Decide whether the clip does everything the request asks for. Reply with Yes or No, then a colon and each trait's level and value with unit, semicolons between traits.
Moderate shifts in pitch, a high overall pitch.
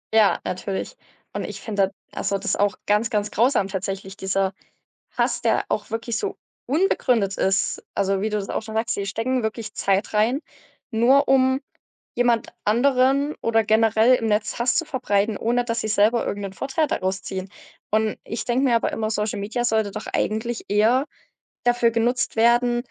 Yes: average, 3.1 semitones; high, 220 Hz